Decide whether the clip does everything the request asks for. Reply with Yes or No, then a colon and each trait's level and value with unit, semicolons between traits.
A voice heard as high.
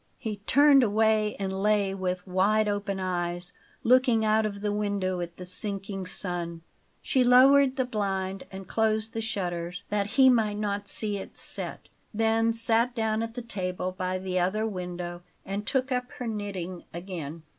Yes: high, 205 Hz